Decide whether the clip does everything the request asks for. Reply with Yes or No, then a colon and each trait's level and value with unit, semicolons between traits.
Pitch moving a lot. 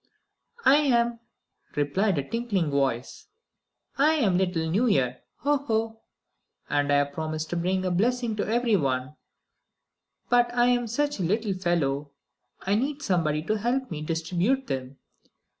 Yes: wide, 7.9 semitones